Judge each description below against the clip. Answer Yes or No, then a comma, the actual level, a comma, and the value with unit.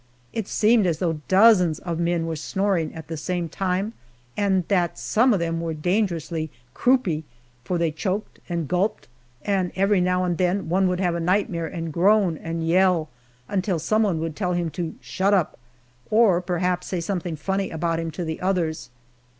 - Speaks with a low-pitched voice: No, medium, 180 Hz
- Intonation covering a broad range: No, average, 2.8 semitones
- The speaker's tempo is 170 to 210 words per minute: Yes, average, 180 wpm